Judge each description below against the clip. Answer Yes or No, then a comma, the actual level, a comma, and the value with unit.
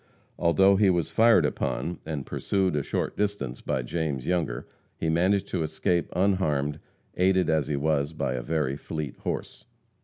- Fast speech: No, average, 160 wpm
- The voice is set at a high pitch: No, very low, 80 Hz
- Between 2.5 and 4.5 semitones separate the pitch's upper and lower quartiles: Yes, average, 4.2 semitones